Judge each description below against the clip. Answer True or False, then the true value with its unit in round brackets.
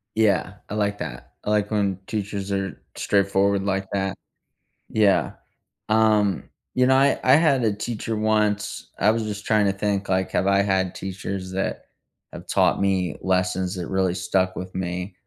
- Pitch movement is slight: True (2.1 semitones)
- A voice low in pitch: True (100 Hz)